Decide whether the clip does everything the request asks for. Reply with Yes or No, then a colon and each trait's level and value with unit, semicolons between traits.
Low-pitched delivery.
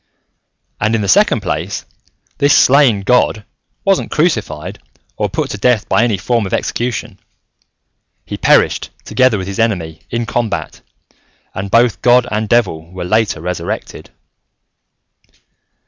Yes: low, 110 Hz